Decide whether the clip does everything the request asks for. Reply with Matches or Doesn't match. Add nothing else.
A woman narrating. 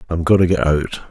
Doesn't match